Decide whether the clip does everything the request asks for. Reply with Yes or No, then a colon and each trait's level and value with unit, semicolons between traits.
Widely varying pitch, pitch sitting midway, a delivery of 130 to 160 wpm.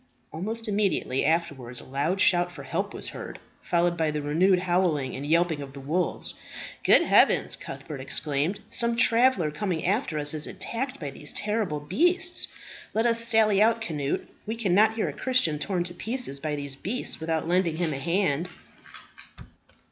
No: wide, 6.3 semitones; medium, 175 Hz; average, 170 wpm